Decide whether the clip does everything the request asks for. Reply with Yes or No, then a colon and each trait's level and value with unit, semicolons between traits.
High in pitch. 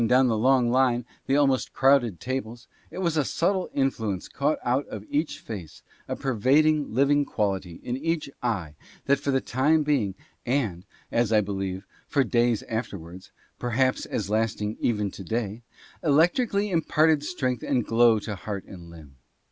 No: low, 120 Hz